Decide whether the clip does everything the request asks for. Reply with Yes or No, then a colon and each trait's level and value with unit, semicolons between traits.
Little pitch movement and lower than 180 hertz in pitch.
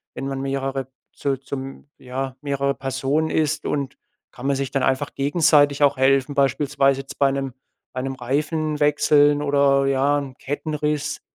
Yes: narrow, 1.3 semitones; medium, 140 Hz